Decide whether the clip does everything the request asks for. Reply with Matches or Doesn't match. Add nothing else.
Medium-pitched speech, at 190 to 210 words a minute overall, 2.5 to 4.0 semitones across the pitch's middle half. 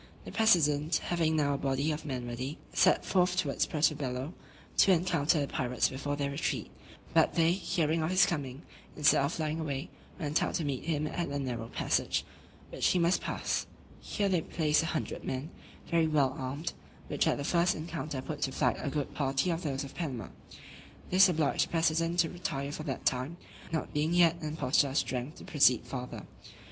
Matches